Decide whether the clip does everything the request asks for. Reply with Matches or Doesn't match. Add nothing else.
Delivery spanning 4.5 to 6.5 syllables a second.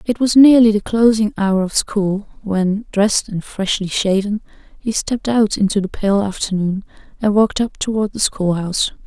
Matches